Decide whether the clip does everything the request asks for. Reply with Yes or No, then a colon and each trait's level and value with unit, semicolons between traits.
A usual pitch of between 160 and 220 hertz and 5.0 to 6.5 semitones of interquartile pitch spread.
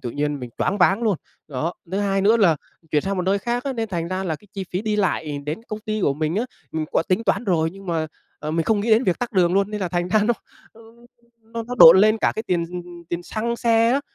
No: high, 190 Hz; average, 4.4 semitones